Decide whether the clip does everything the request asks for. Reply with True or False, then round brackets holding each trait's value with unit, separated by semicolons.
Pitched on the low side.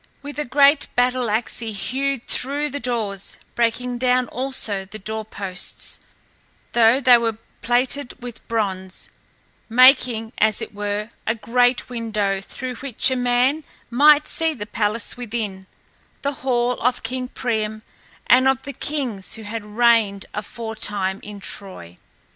False (235 Hz)